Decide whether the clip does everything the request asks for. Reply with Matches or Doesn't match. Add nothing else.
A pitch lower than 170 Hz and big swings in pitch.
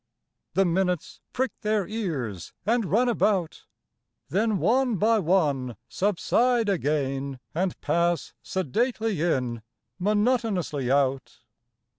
Doesn't match